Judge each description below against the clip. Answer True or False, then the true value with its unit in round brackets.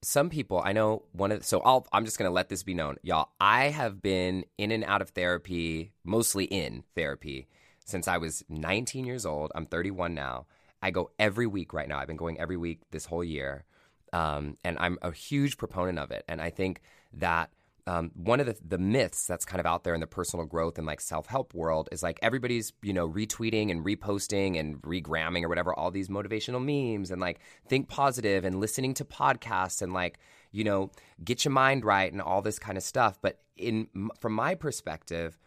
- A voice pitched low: True (95 Hz)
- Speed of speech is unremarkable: False (210 wpm)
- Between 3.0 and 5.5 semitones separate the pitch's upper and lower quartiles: True (4.9 semitones)